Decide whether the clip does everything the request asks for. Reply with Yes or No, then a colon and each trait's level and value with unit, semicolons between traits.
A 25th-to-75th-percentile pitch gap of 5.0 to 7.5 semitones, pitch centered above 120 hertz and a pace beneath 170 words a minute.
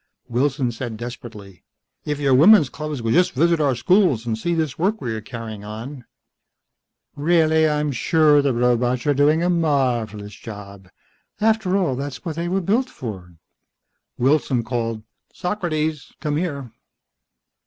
Yes: average, 5.3 semitones; medium, 140 Hz; average, 150 wpm